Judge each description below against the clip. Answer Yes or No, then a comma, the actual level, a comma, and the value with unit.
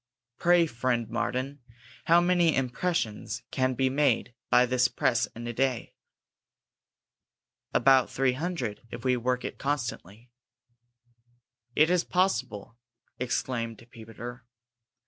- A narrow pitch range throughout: No, average, 3.5 semitones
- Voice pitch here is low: Yes, low, 125 Hz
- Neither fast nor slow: No, slow, 110 wpm